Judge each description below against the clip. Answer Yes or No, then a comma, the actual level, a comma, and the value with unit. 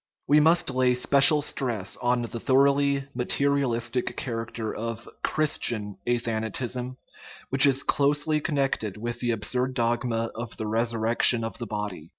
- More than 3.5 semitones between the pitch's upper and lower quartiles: No, average, 3.2 semitones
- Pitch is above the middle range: No, low, 120 Hz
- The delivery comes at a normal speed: Yes, average, 150 wpm